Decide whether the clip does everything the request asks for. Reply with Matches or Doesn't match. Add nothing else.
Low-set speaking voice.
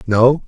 Matches